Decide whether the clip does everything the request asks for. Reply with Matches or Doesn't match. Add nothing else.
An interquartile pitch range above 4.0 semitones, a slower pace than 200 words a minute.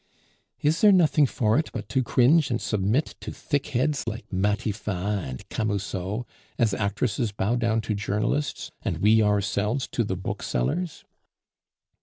Matches